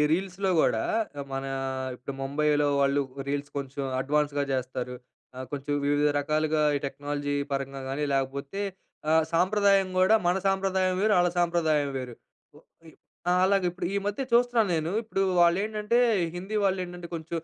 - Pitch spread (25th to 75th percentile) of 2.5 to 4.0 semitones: No, average, 5.2 semitones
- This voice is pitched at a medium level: Yes, medium, 155 Hz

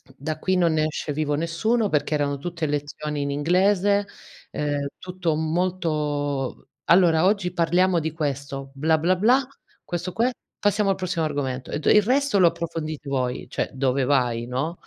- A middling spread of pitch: Yes, average, 4.1 semitones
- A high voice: No, medium, 160 Hz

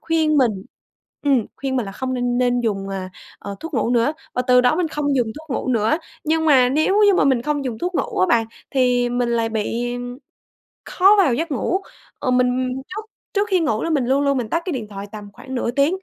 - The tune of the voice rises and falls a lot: No, average, 4.6 semitones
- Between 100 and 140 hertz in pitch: No, very high, 255 Hz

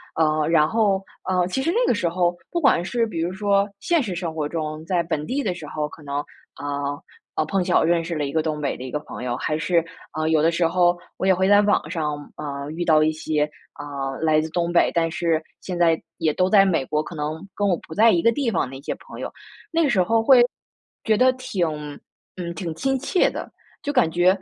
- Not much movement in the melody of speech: No, average, 4.1 semitones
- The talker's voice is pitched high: No, medium, 170 Hz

